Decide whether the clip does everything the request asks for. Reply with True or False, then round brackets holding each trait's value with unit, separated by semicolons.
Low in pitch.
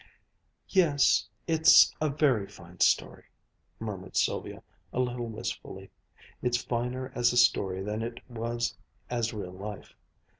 True (120 Hz)